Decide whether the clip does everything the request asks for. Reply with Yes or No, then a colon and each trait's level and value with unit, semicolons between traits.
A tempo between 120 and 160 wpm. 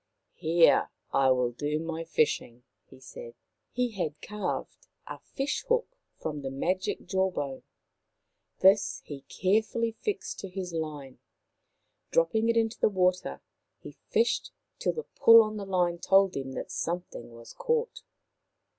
Yes: average, 150 wpm